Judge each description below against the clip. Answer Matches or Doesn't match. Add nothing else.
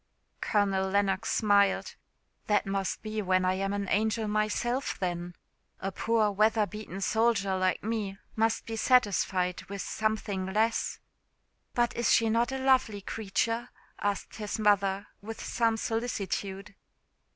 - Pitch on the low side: Doesn't match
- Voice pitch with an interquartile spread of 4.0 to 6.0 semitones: Doesn't match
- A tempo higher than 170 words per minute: Doesn't match